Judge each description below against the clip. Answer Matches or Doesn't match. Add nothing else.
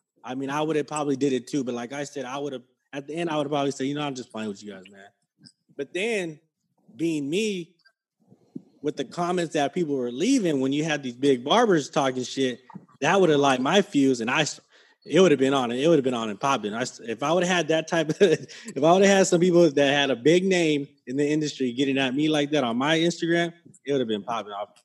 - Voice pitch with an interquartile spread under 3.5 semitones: Doesn't match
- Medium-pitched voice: Matches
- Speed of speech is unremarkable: Doesn't match